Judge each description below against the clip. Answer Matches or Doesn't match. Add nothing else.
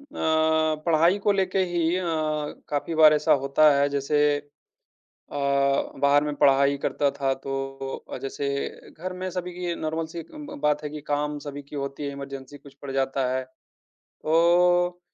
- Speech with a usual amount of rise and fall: Matches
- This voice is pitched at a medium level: Matches